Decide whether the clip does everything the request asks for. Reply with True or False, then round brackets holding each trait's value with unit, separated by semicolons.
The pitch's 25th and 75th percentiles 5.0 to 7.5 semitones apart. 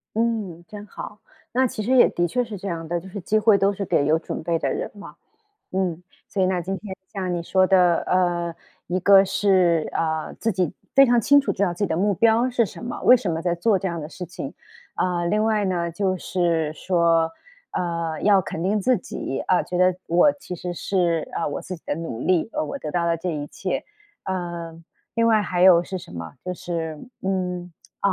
False (3.1 semitones)